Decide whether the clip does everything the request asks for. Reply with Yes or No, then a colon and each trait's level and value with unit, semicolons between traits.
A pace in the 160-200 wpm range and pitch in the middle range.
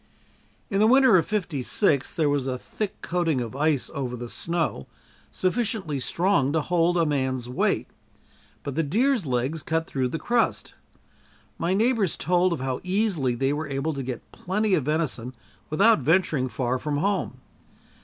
Yes: average, 165 wpm; medium, 160 Hz